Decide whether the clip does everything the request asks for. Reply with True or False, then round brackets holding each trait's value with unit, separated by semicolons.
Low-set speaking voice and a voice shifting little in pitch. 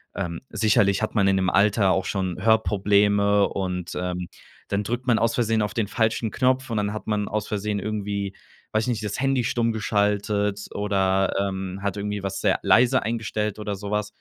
True (105 Hz; 1.9 semitones)